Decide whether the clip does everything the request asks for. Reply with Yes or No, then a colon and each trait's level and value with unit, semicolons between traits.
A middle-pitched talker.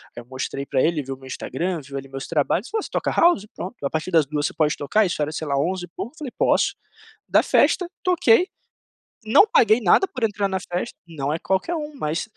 Yes: medium, 175 Hz